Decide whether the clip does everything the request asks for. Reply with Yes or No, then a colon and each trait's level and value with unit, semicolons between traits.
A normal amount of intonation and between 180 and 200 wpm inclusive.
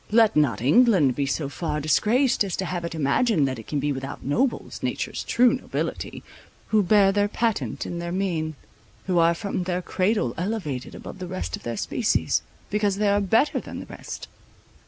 No: wide, 6.2 semitones; average, 190 wpm